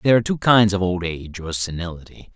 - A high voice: No, very low, 95 Hz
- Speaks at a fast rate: Yes, fast, 230 wpm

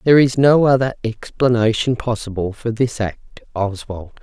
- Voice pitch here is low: Yes, low, 115 Hz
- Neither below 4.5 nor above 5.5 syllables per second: Yes, 4.8 syllables/s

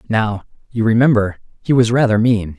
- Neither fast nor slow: Yes, average, 160 wpm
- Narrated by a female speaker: No, male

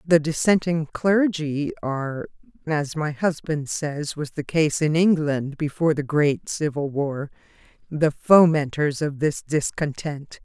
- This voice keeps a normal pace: No, slow, 130 wpm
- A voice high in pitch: No, medium, 155 Hz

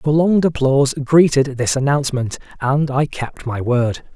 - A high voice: No, medium, 140 Hz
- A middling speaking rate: Yes, average, 145 wpm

